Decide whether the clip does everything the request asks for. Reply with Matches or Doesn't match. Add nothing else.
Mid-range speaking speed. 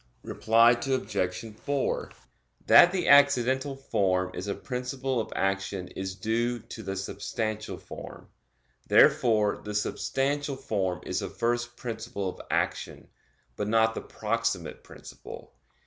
Doesn't match